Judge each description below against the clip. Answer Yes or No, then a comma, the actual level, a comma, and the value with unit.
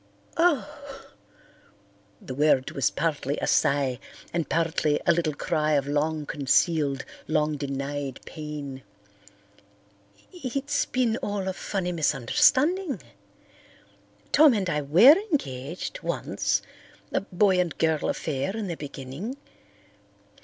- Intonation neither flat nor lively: No, wide, 6.7 semitones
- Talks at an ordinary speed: No, slow, 110 wpm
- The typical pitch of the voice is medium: Yes, medium, 160 Hz